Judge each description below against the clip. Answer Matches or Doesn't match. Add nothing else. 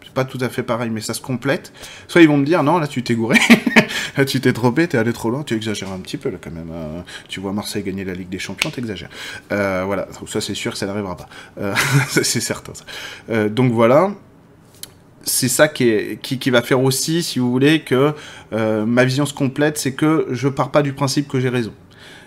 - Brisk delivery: Matches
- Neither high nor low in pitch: Doesn't match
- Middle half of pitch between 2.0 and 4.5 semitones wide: Doesn't match